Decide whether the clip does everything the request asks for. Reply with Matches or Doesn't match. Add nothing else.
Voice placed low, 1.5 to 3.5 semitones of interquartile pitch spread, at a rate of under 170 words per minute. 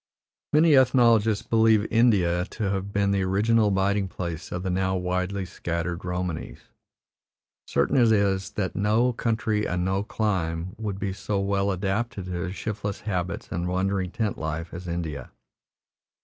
Matches